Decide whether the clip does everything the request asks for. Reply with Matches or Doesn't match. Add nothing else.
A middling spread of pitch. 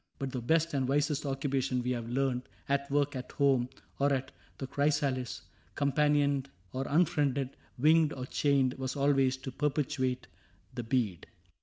Doesn't match